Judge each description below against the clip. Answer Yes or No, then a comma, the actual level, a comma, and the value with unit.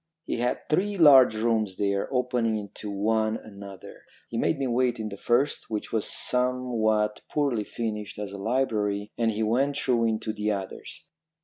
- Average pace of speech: Yes, average, 170 wpm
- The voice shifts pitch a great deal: No, average, 3.1 semitones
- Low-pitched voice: Yes, low, 110 Hz